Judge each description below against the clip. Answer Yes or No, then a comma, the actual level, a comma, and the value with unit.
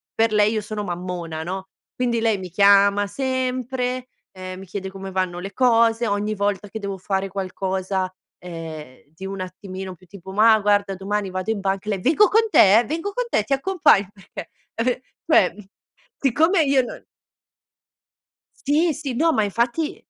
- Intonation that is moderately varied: Yes, average, 4.5 semitones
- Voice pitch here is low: No, high, 205 Hz